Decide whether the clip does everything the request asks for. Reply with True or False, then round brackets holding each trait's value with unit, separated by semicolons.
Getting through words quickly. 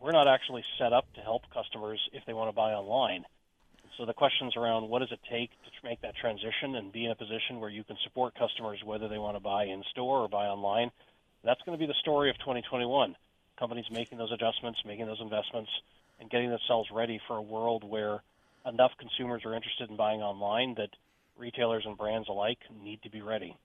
True (215 wpm)